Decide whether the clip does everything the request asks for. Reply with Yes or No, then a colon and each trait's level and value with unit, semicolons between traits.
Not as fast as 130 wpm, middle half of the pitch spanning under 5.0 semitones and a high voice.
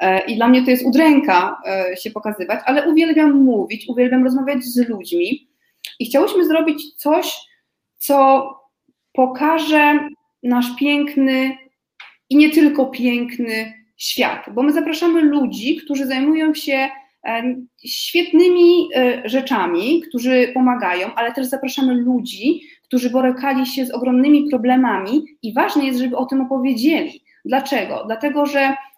Yes: average, 120 wpm; average, 3.1 semitones; very high, 270 Hz